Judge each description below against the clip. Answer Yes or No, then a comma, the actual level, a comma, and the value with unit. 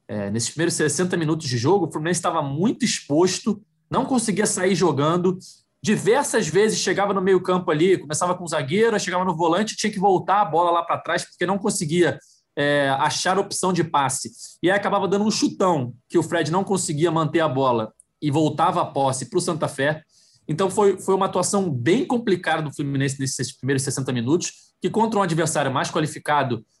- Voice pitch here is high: No, medium, 175 Hz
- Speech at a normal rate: No, fast, 195 wpm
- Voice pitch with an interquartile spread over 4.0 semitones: Yes, average, 4.4 semitones